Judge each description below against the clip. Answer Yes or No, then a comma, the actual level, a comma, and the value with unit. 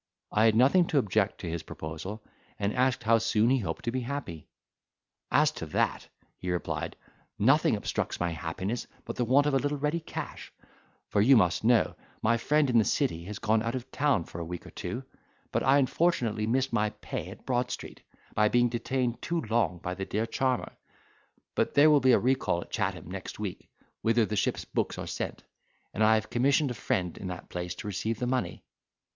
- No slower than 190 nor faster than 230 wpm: Yes, fast, 205 wpm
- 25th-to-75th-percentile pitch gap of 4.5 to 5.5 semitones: Yes, average, 4.8 semitones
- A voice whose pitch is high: No, low, 115 Hz